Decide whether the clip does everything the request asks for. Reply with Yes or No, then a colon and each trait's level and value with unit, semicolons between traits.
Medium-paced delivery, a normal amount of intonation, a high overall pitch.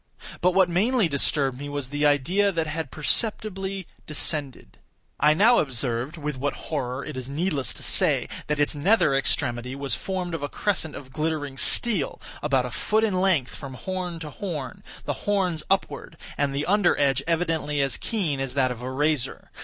No: average, 175 wpm; average, 4.9 semitones; medium, 150 Hz